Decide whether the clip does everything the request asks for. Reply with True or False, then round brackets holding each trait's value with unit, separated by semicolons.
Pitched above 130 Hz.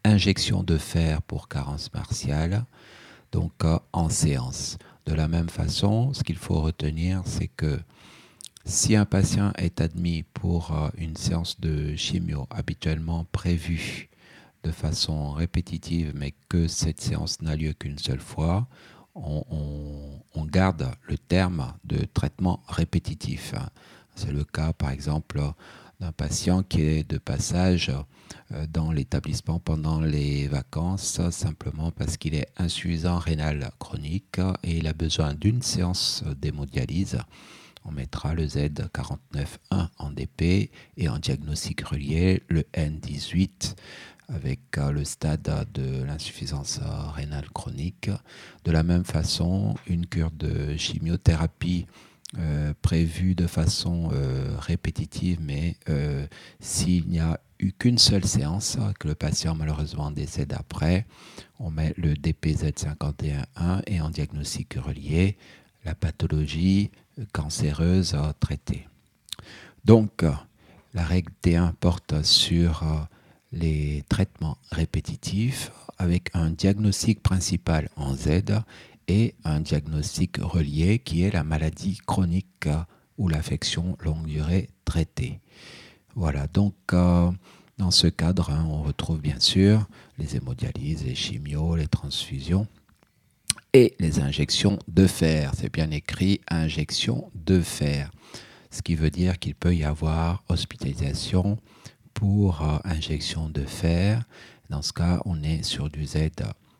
False (85 Hz)